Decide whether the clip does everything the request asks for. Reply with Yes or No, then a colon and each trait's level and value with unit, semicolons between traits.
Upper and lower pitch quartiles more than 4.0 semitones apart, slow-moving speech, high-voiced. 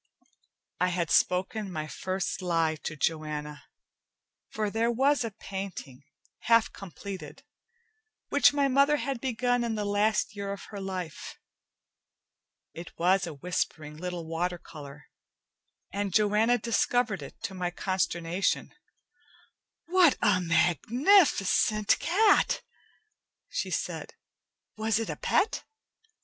Yes: average, 4.9 semitones; slow, 115 wpm; high, 195 Hz